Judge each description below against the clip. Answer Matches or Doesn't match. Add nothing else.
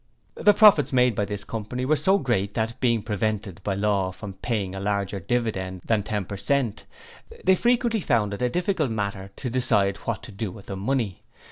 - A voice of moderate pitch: Doesn't match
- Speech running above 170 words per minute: Matches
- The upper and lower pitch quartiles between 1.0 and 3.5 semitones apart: Doesn't match